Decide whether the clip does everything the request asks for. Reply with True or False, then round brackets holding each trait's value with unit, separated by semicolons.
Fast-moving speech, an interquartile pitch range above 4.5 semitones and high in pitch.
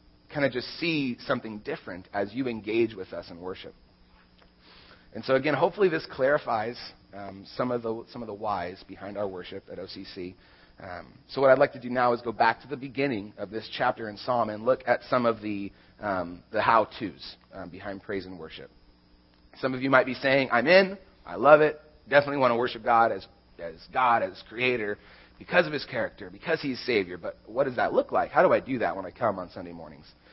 False (220 wpm; 5.6 semitones; 115 Hz)